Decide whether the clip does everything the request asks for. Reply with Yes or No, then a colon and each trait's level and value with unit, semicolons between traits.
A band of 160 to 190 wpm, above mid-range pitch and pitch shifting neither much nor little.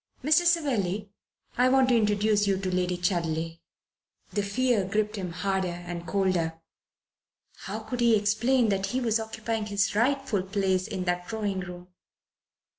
No: average, 150 wpm; high, 205 Hz; average, 3.6 semitones